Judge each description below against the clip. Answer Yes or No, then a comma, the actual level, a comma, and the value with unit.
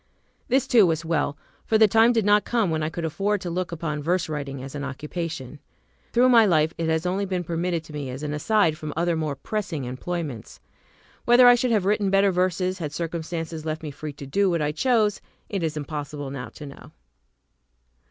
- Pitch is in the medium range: Yes, medium, 165 Hz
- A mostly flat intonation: No, average, 4.8 semitones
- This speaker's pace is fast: Yes, fast, 210 wpm